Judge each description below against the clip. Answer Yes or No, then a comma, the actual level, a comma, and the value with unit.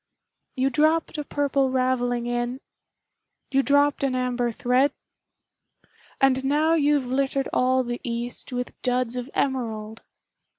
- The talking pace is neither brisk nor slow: No, slow, 125 wpm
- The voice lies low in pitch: No, very high, 260 Hz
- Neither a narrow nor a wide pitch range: No, narrow, 2.2 semitones